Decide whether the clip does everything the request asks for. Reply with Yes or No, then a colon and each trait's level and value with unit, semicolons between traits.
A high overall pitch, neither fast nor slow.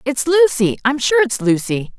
Yes: high, 230 Hz; average, 150 wpm